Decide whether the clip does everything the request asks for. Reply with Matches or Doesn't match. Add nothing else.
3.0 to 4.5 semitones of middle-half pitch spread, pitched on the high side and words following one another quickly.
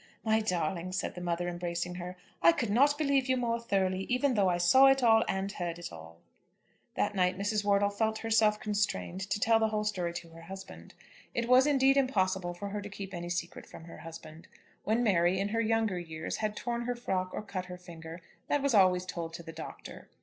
Matches